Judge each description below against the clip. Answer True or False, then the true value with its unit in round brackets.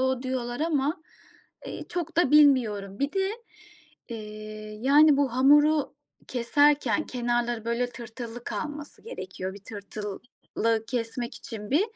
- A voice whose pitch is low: False (250 Hz)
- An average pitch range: True (4.5 semitones)